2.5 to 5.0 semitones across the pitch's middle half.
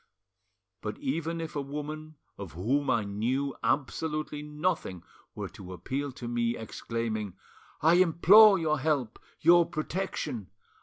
No: wide, 5.6 semitones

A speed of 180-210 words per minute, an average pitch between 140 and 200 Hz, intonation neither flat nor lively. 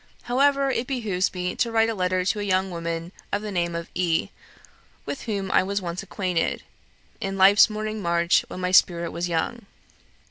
Yes: average, 185 wpm; high, 190 Hz; average, 3.7 semitones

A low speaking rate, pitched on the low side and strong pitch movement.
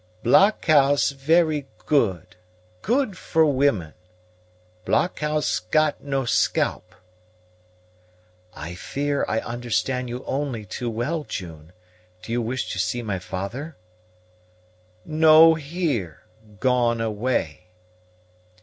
Yes: slow, 95 wpm; low, 130 Hz; wide, 6.0 semitones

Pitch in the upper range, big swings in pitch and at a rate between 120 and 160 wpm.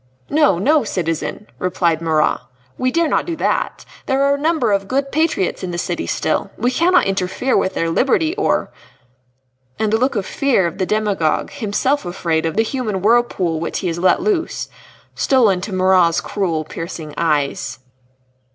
No: high, 195 Hz; wide, 8.0 semitones; average, 175 wpm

